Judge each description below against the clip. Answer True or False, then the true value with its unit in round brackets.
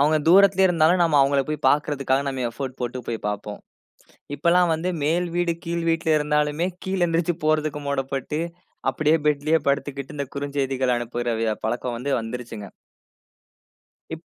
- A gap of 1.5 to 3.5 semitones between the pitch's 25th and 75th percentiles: False (3.9 semitones)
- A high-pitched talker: False (145 Hz)